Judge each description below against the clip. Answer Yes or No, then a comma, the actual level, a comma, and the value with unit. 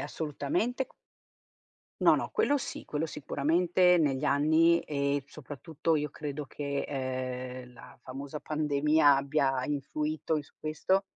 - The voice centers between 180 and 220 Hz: No, medium, 150 Hz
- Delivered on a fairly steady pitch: Yes, narrow, 2.3 semitones